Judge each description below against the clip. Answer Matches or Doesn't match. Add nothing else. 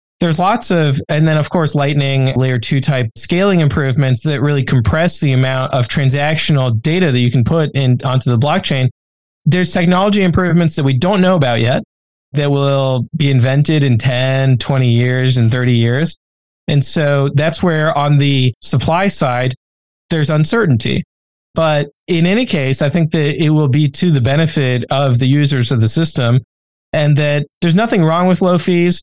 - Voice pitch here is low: Doesn't match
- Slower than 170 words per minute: Doesn't match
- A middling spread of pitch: Matches